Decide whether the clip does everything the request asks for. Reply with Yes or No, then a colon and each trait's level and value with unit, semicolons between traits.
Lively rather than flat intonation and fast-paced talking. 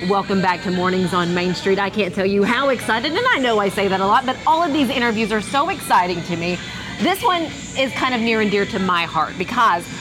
Yes: wide, 6.3 semitones; fast, 260 wpm